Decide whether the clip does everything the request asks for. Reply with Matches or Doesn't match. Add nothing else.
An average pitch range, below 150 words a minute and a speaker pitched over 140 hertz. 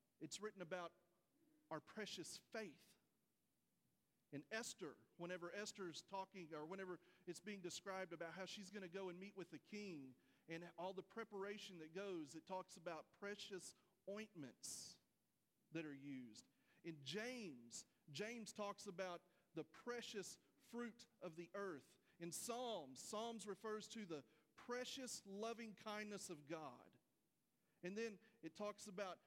Matches